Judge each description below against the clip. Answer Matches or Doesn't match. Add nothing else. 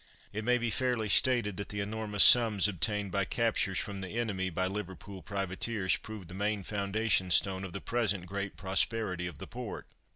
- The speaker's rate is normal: Matches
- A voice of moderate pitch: Doesn't match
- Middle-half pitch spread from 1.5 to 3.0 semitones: Matches